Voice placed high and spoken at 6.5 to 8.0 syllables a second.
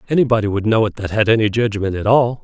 No: low, 110 Hz; 6.7 syllables/s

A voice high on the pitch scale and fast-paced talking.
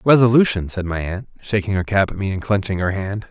No: low, 100 Hz; fast, 255 wpm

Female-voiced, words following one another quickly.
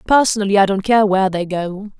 Yes: female; fast, 210 wpm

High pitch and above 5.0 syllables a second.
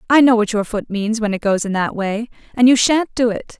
Yes: high, 225 Hz; 5.5 syllables/s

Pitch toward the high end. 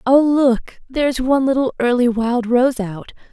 Yes: very high, 250 Hz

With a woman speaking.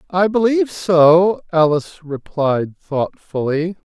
No: male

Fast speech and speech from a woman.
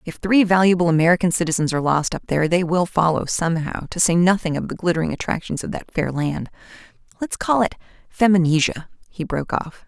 No: average, 175 wpm; female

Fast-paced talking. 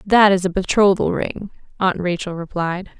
No: average, 160 wpm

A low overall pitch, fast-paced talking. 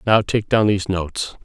Yes: low, 100 Hz; fast, 210 wpm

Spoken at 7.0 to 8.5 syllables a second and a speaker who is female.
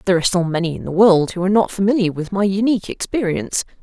Yes: 7.4 syllables/s; female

